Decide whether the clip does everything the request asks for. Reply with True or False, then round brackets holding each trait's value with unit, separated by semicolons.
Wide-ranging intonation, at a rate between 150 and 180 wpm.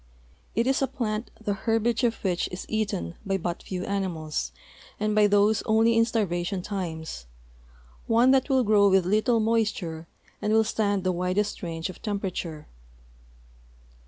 False (3.6 semitones; 155 wpm)